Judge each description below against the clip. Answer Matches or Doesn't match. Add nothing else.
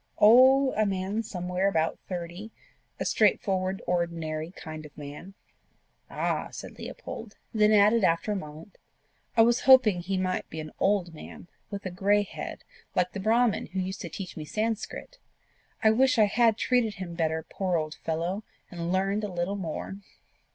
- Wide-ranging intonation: Doesn't match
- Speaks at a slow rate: Doesn't match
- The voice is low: Doesn't match